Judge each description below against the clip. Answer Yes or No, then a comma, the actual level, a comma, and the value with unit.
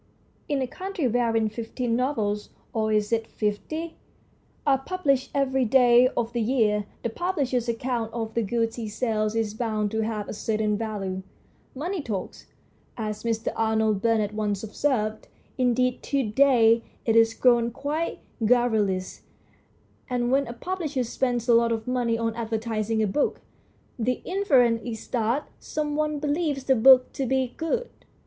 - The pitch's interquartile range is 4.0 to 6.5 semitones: No, average, 3.3 semitones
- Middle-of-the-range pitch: No, high, 235 Hz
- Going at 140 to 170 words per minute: Yes, average, 155 wpm